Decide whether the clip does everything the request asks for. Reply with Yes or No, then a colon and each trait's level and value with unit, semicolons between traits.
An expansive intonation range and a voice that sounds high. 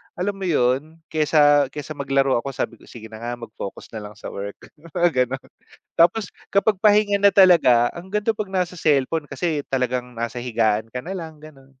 No: wide, 6.4 semitones; medium, 145 Hz